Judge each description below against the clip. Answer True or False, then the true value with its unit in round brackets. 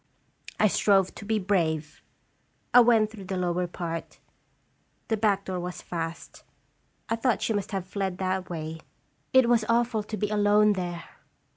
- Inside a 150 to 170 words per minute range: True (160 wpm)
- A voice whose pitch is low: False (195 Hz)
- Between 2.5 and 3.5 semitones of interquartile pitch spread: True (3.2 semitones)